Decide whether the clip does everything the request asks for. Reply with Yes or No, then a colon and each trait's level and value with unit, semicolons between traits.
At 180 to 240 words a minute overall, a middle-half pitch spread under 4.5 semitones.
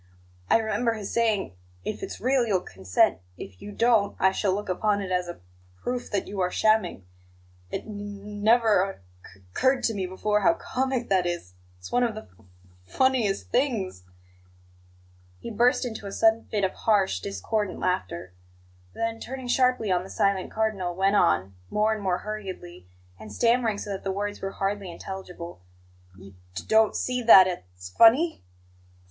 Yes: average, 185 wpm; average, 3.9 semitones